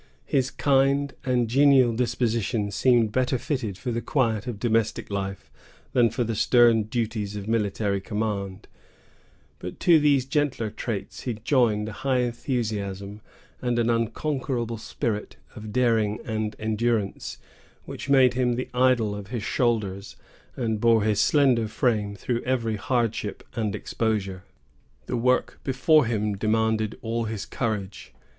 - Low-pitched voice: Yes, low, 115 Hz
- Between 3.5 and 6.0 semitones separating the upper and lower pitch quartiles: No, average, 3.0 semitones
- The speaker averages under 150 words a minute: Yes, average, 140 wpm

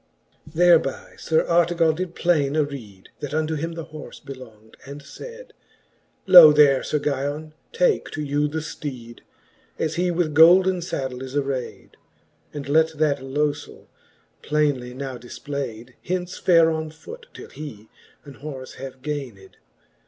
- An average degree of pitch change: Yes, average, 3.2 semitones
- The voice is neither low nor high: Yes, medium, 150 Hz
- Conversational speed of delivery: Yes, average, 145 wpm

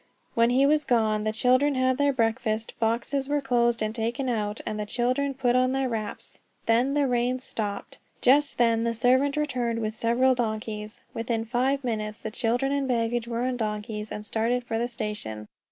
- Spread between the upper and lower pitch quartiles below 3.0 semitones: Yes, narrow, 2.6 semitones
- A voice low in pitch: No, high, 235 Hz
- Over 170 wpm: Yes, average, 185 wpm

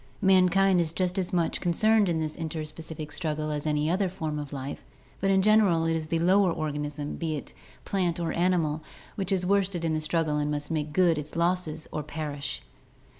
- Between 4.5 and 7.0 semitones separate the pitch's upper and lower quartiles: No, average, 3.1 semitones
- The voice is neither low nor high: Yes, medium, 165 Hz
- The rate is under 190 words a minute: No, average, 195 wpm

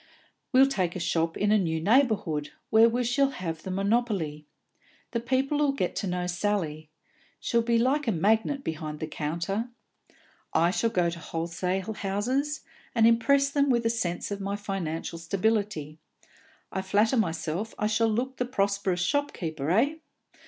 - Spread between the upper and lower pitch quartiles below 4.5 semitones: No, wide, 5.6 semitones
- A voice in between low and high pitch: No, high, 205 Hz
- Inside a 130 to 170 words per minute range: Yes, average, 165 wpm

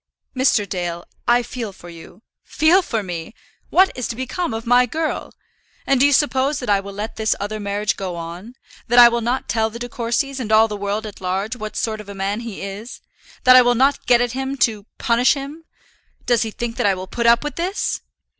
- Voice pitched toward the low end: No, high, 230 Hz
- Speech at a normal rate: No, fast, 230 wpm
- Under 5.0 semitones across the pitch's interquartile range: Yes, average, 3.9 semitones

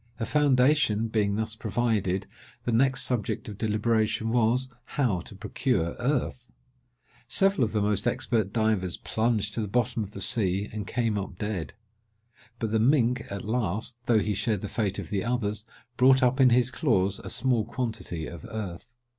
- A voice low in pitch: Yes, low, 110 Hz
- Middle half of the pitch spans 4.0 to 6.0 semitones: No, average, 3.2 semitones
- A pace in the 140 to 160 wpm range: No, average, 170 wpm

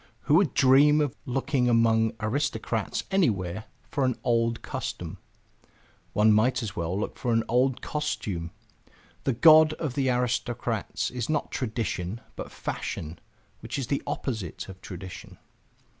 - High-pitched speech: No, low, 120 Hz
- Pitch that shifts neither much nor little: Yes, average, 3.8 semitones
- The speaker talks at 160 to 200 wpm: No, average, 140 wpm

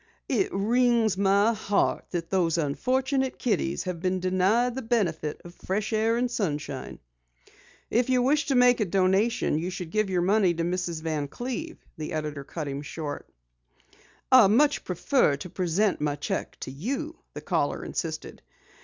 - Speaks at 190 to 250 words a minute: No, average, 165 wpm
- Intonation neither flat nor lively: No, wide, 6.5 semitones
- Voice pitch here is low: No, high, 195 Hz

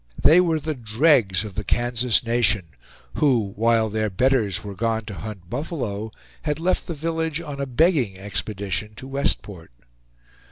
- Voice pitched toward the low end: Yes, low, 115 Hz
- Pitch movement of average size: No, wide, 5.8 semitones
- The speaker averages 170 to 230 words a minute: No, average, 155 wpm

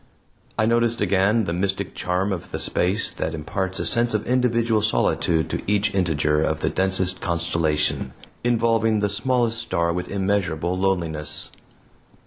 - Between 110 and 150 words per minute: Yes, average, 140 wpm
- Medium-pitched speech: No, very low, 95 Hz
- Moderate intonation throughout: Yes, average, 4.6 semitones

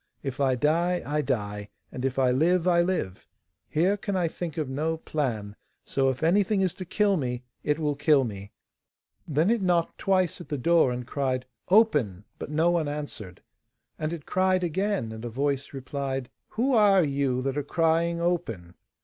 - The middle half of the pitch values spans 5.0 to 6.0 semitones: Yes, average, 5.3 semitones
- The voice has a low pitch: No, medium, 150 Hz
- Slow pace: No, average, 185 wpm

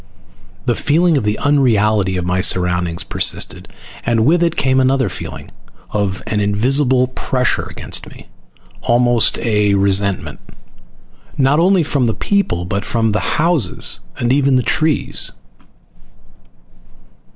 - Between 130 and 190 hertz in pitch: No, low, 120 Hz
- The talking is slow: Yes, slow, 130 wpm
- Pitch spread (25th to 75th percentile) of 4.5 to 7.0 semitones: Yes, wide, 5.5 semitones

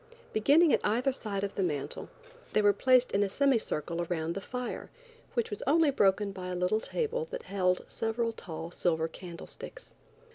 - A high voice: Yes, high, 205 Hz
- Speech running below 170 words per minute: No, average, 180 wpm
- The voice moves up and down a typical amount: No, wide, 5.8 semitones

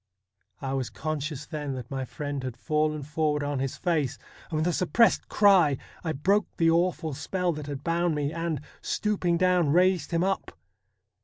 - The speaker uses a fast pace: No, average, 175 wpm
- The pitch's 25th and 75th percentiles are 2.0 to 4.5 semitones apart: Yes, average, 3.4 semitones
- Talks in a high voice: No, medium, 155 Hz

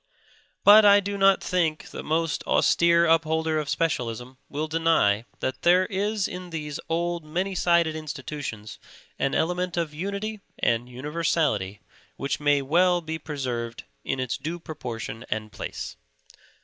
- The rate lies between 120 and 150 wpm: Yes, average, 140 wpm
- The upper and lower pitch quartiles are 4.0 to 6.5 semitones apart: Yes, average, 4.4 semitones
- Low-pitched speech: No, medium, 160 Hz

